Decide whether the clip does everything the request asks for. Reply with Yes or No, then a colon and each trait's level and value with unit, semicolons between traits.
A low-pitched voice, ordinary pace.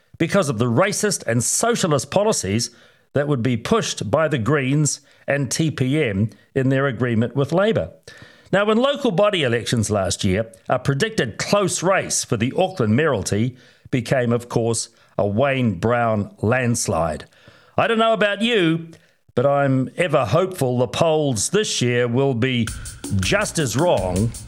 Yes: low, 130 Hz; average, 150 wpm